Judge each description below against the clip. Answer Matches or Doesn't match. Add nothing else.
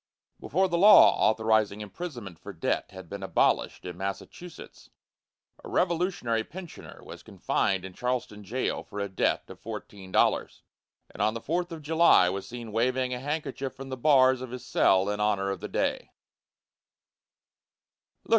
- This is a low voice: Matches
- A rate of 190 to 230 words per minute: Doesn't match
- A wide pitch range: Matches